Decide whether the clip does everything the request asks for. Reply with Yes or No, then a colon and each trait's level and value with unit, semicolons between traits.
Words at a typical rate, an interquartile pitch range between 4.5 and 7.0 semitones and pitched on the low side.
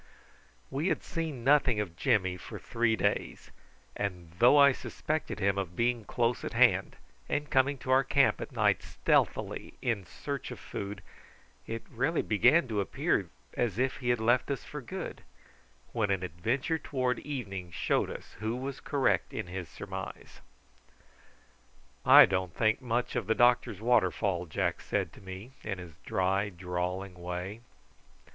Yes: average, 155 wpm; wide, 5.6 semitones; low, 110 Hz